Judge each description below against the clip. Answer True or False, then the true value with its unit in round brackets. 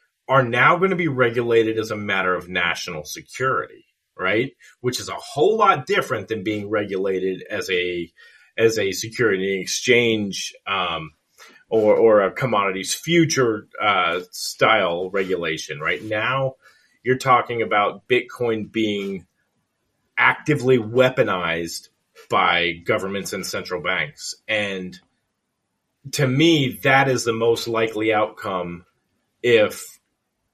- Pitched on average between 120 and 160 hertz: False (110 Hz)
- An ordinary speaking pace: False (120 wpm)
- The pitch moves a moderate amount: False (5.8 semitones)